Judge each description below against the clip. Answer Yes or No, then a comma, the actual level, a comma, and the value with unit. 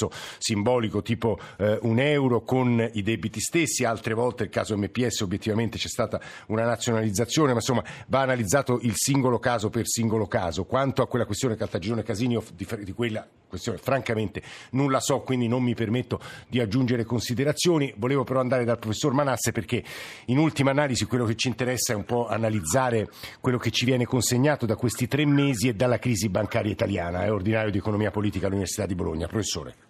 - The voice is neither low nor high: No, low, 115 Hz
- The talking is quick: Yes, fast, 185 wpm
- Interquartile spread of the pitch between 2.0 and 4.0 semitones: Yes, average, 2.9 semitones